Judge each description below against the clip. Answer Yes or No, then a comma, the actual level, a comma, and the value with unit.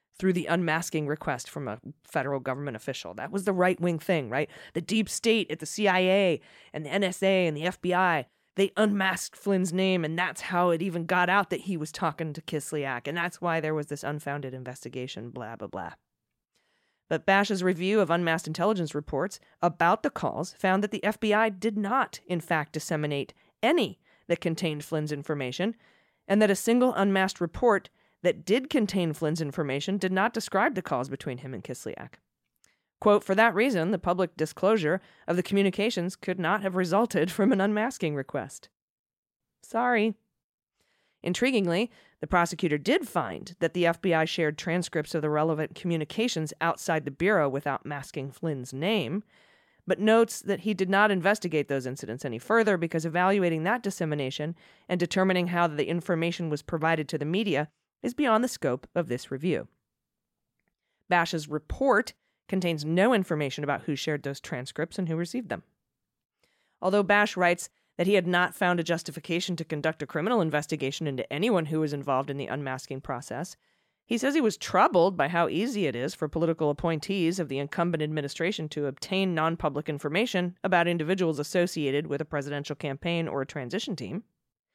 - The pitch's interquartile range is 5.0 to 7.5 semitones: No, average, 4.2 semitones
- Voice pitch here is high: No, medium, 170 Hz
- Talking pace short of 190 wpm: Yes, average, 170 wpm